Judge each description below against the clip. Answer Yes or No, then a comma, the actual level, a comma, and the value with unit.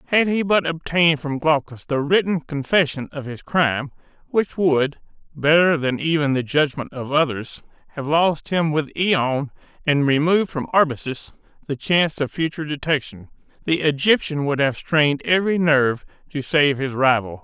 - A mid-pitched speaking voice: Yes, medium, 150 Hz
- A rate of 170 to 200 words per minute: No, average, 160 wpm